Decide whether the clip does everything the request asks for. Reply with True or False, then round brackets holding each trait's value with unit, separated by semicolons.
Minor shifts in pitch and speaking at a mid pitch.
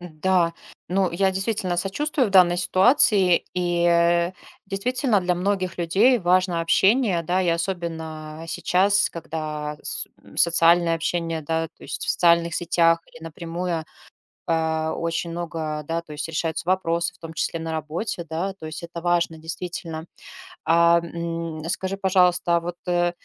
True (1.9 semitones; 170 Hz)